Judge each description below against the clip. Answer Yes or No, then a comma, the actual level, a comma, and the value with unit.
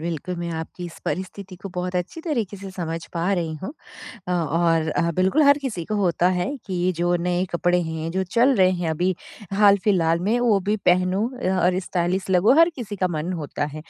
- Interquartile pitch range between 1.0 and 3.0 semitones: Yes, narrow, 2.6 semitones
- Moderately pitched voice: Yes, medium, 180 Hz